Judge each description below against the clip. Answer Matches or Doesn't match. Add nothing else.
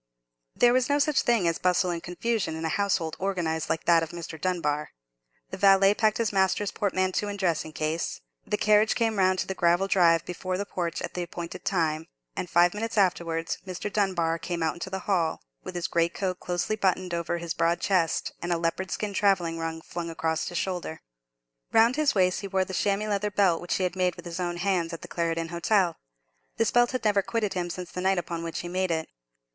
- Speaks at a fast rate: Matches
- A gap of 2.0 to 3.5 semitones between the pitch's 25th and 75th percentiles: Matches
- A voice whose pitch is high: Doesn't match